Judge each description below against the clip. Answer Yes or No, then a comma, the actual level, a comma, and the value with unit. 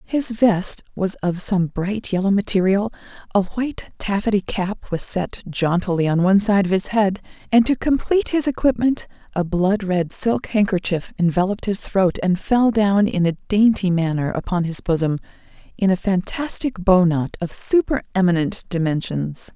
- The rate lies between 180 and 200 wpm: No, average, 165 wpm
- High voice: Yes, high, 195 Hz